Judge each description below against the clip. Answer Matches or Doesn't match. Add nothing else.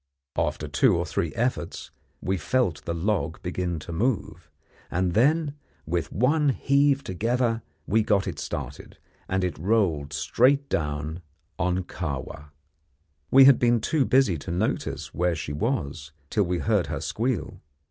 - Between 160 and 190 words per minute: Doesn't match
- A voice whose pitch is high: Doesn't match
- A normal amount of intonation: Doesn't match